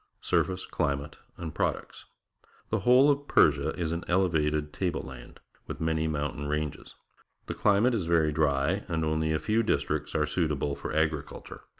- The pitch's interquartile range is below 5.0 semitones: Yes, average, 3.5 semitones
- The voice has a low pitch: Yes, very low, 80 Hz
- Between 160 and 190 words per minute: Yes, average, 170 wpm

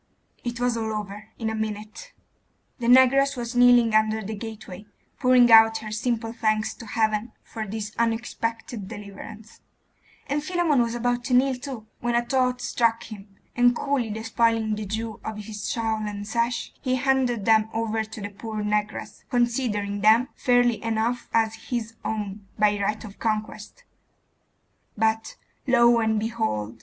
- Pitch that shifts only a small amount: Yes, narrow, 2.1 semitones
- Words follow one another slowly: No, average, 155 wpm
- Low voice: No, high, 225 Hz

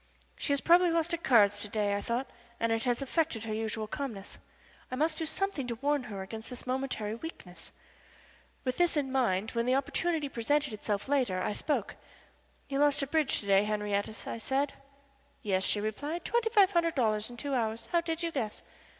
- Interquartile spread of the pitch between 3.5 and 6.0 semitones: Yes, wide, 5.6 semitones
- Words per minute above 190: Yes, average, 200 wpm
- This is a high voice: Yes, very high, 255 Hz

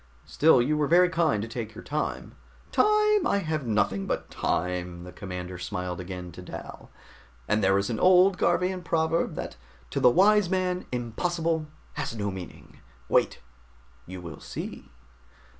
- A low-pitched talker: Yes, low, 125 Hz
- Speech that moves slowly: No, average, 160 wpm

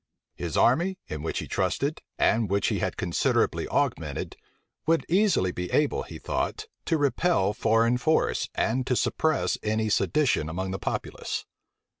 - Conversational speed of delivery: Yes, average, 150 wpm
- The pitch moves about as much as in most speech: No, wide, 8.4 semitones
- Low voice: Yes, low, 120 Hz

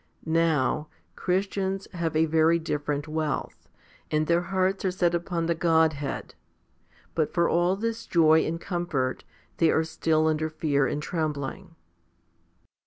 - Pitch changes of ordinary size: No, narrow, 2.0 semitones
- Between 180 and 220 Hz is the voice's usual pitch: No, medium, 160 Hz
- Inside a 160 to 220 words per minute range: No, slow, 135 wpm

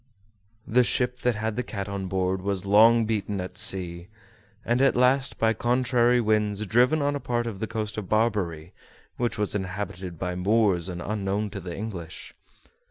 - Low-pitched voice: Yes, low, 105 Hz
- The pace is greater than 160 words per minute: Yes, average, 170 wpm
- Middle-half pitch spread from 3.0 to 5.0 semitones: Yes, average, 3.7 semitones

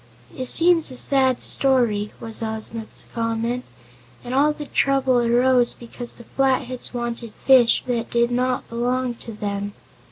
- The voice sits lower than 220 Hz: No, high, 245 Hz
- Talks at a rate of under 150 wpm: Yes, average, 140 wpm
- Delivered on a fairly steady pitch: Yes, narrow, 2.0 semitones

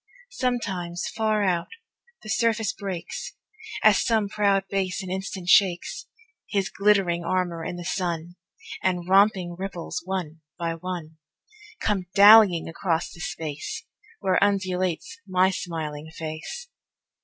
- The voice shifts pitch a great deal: No, average, 2.8 semitones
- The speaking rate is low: Yes, slow, 120 wpm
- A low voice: No, medium, 185 Hz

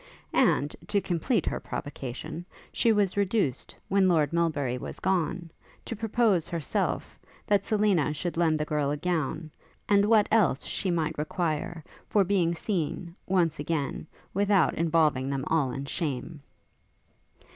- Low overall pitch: No, medium, 170 Hz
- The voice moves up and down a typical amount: Yes, average, 4.5 semitones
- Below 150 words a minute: Yes, average, 140 wpm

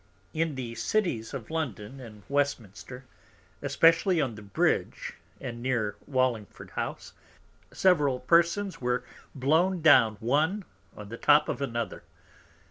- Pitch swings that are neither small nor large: No, wide, 5.7 semitones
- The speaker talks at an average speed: No, slow, 125 wpm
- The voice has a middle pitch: No, low, 130 Hz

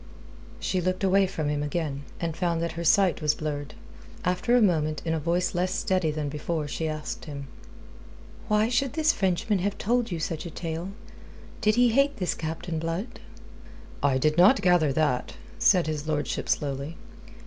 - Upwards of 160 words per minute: Yes, average, 175 wpm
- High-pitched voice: No, medium, 170 Hz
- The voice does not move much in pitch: No, average, 3.9 semitones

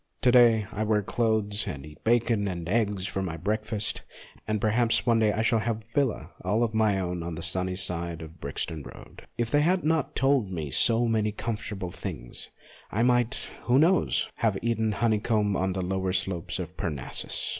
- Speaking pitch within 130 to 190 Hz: No, low, 105 Hz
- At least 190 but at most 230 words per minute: Yes, fast, 205 wpm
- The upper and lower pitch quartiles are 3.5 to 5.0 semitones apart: Yes, average, 4.0 semitones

